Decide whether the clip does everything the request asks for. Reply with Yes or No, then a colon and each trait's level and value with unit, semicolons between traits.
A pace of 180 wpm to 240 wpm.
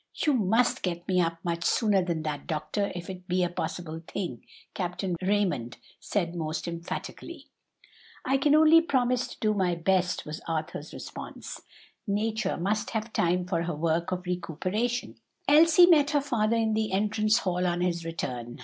No: average, 165 wpm